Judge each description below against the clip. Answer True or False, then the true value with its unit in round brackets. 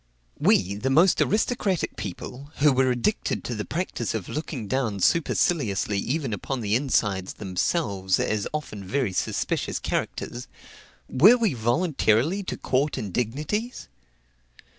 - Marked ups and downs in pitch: True (7.0 semitones)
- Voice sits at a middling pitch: False (130 Hz)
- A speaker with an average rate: False (130 wpm)